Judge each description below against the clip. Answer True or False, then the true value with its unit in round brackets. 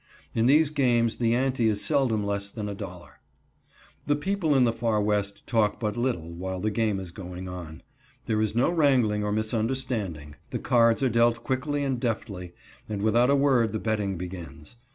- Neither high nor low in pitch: False (110 Hz)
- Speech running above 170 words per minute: True (180 wpm)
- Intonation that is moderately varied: True (3.9 semitones)